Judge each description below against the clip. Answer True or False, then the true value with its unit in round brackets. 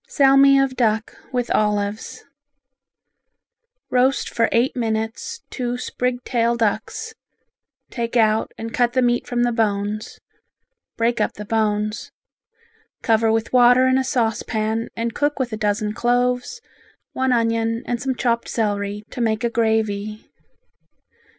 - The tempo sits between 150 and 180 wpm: False (135 wpm)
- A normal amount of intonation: False (2.3 semitones)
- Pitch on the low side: False (230 Hz)